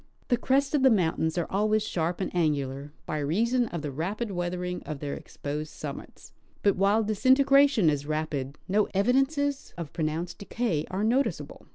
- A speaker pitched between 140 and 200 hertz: Yes, medium, 185 Hz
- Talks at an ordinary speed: Yes, average, 165 wpm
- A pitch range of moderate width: No, wide, 7.2 semitones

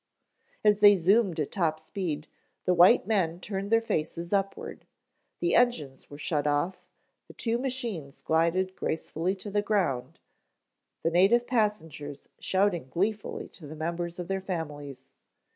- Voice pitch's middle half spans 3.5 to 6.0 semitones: Yes, average, 4.6 semitones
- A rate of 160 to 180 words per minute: No, average, 145 wpm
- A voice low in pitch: No, medium, 180 Hz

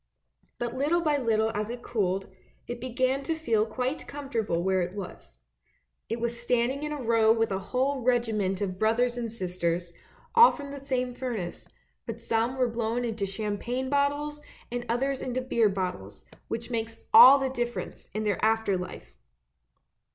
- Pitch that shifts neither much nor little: Yes, average, 3.6 semitones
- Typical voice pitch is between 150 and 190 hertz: No, high, 235 Hz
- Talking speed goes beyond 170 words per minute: No, average, 165 wpm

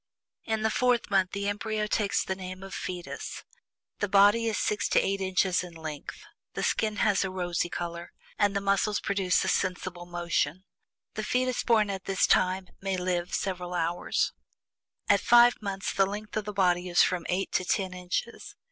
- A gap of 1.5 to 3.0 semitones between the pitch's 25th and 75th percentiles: Yes, narrow, 2.5 semitones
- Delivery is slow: No, average, 185 wpm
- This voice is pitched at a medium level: No, high, 195 Hz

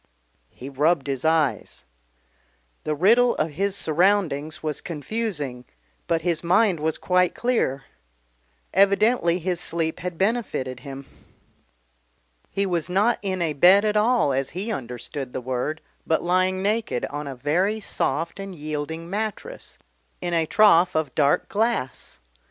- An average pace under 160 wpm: Yes, average, 140 wpm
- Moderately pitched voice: Yes, medium, 170 Hz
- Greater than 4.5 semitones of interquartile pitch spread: Yes, average, 5.2 semitones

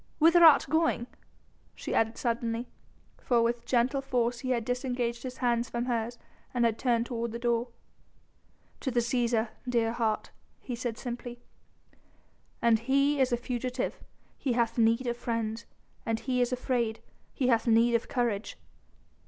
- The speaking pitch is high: Yes, high, 240 Hz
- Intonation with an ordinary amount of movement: No, narrow, 1.4 semitones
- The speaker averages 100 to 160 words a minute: Yes, average, 155 wpm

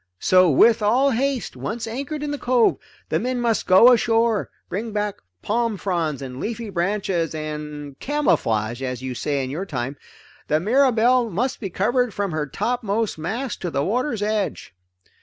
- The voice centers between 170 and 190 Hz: No, high, 210 Hz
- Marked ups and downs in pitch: Yes, wide, 7.5 semitones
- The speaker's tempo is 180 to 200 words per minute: No, average, 155 wpm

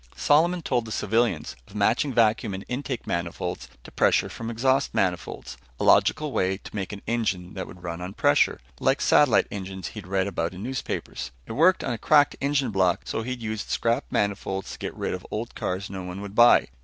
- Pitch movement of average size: Yes, average, 4.6 semitones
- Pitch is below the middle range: Yes, low, 105 Hz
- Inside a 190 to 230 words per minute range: Yes, fast, 205 wpm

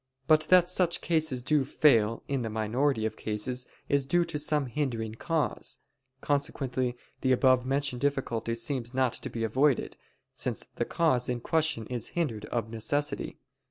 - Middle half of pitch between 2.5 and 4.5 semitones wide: Yes, average, 4.2 semitones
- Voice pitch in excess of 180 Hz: No, low, 130 Hz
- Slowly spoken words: No, average, 160 wpm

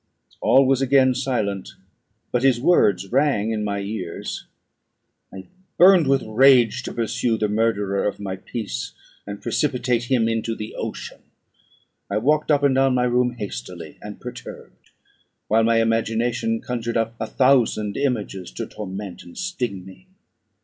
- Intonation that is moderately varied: Yes, average, 4.0 semitones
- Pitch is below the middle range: Yes, low, 115 Hz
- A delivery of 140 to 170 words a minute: Yes, average, 150 wpm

